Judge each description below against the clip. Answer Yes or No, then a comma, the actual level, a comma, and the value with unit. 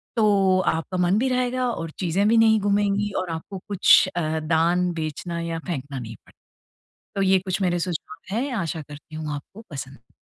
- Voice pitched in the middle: Yes, medium, 180 Hz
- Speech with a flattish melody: No, average, 4.1 semitones